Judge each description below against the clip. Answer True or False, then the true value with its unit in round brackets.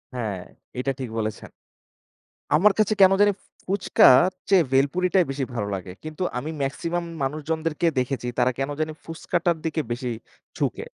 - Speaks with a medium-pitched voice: True (155 Hz)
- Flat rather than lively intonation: False (5.4 semitones)